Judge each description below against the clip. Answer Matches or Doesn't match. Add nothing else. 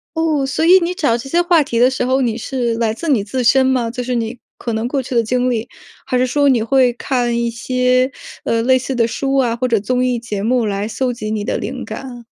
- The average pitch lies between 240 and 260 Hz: Matches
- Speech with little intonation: Matches